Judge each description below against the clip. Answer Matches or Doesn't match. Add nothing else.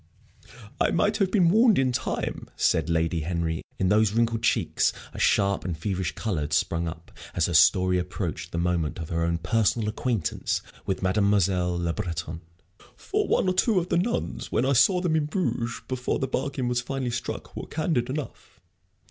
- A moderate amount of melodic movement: Doesn't match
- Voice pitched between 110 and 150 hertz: Doesn't match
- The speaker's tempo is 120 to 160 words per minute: Doesn't match